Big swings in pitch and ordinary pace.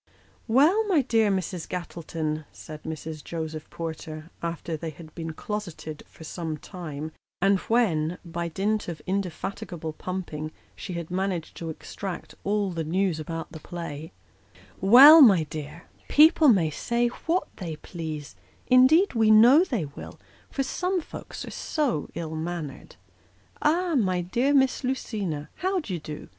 Yes: wide, 6.3 semitones; average, 150 wpm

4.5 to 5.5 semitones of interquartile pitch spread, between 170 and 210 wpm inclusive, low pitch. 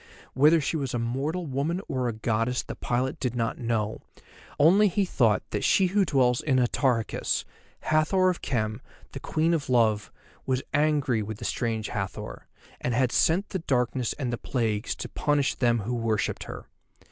Yes: average, 4.9 semitones; average, 175 wpm; low, 125 Hz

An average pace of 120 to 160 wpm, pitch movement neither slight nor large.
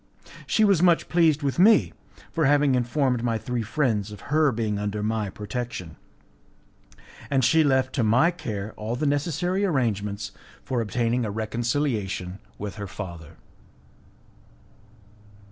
No: slow, 135 wpm; wide, 5.8 semitones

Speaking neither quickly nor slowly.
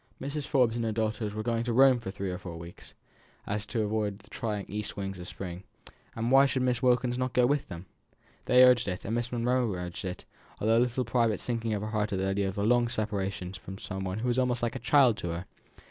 No: fast, 250 wpm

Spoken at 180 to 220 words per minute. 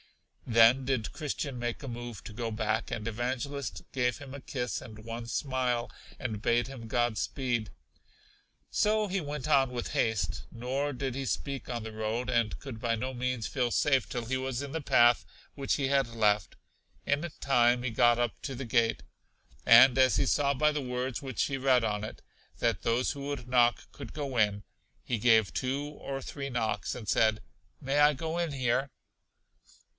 Yes: average, 190 wpm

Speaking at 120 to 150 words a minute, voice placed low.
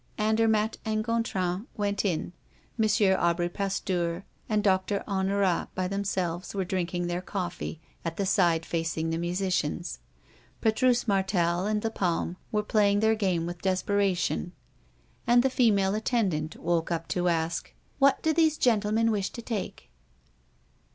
No: average, 140 wpm; high, 195 Hz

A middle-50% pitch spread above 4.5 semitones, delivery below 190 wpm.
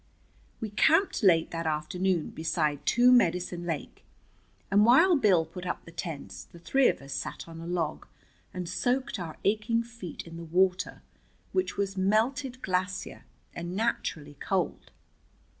Yes: wide, 5.4 semitones; average, 150 wpm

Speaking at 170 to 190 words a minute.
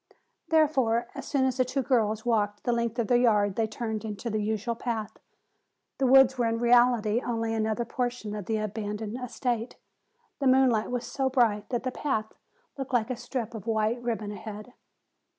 Yes: average, 185 wpm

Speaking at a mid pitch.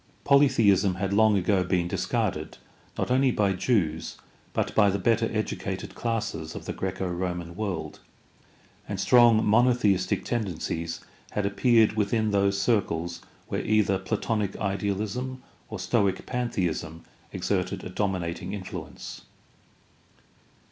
No: low, 100 Hz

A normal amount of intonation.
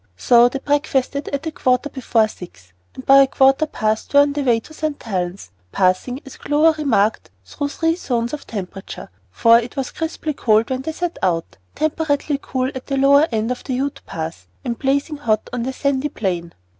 Yes: average, 4.5 semitones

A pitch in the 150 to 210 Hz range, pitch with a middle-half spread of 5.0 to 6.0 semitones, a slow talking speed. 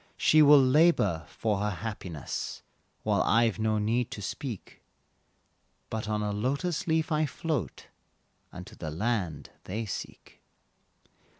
No: low, 110 Hz; wide, 5.5 semitones; slow, 125 wpm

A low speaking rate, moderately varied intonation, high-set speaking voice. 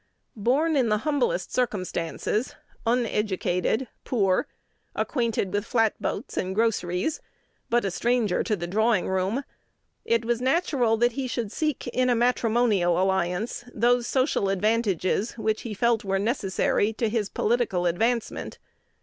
Yes: slow, 130 wpm; average, 3.8 semitones; high, 225 Hz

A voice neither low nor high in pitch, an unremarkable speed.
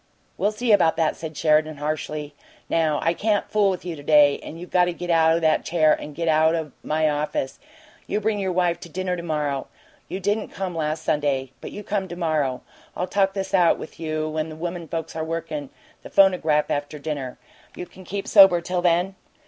No: medium, 165 Hz; fast, 215 wpm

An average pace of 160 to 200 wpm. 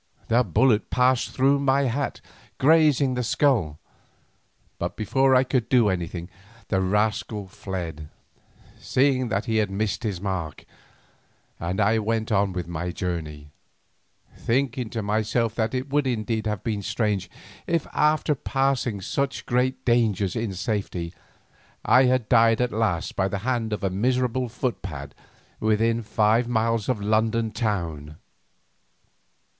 No: average, 140 wpm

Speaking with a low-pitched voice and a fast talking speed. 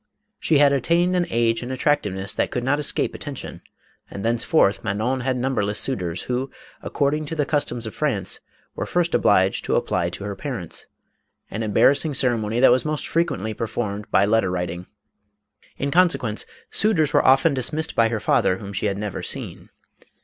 No: low, 120 Hz; average, 180 wpm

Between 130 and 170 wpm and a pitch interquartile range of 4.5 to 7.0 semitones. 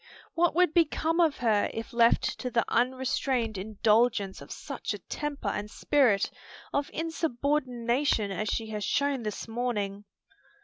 Yes: average, 140 wpm; average, 4.9 semitones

